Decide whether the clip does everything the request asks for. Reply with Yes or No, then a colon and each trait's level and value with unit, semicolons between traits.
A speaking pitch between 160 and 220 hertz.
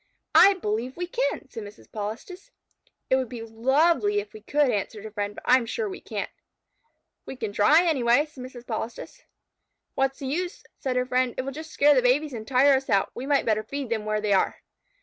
No: very high, 255 Hz